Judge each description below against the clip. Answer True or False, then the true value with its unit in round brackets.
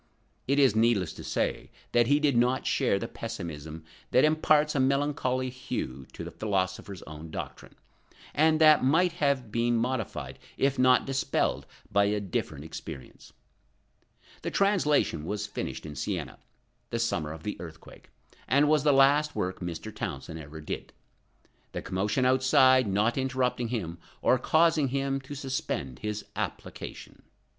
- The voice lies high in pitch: False (125 Hz)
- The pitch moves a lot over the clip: True (6.8 semitones)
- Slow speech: False (150 wpm)